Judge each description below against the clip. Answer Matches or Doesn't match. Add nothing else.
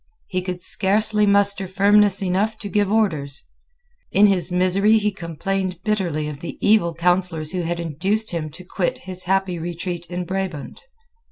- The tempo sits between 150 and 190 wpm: Matches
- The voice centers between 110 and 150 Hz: Doesn't match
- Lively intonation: Doesn't match